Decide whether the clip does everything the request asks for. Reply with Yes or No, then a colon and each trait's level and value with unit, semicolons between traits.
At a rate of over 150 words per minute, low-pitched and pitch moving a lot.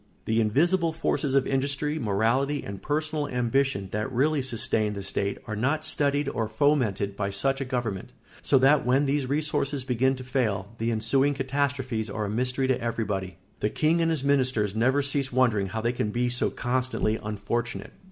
No: average, 180 wpm; low, 130 Hz; average, 4.3 semitones